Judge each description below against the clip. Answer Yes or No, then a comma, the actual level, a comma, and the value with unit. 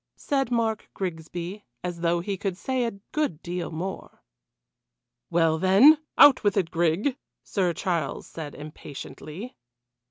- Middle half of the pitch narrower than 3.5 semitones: No, average, 4.7 semitones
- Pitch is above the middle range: No, medium, 180 Hz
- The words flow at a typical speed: No, slow, 130 wpm